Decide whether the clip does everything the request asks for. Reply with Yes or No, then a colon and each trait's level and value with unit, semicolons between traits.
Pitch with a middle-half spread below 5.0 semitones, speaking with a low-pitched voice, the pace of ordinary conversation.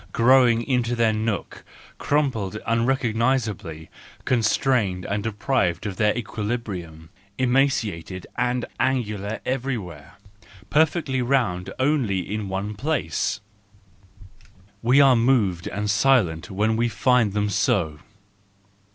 No: average, 4.5 semitones; low, 110 Hz; slow, 100 wpm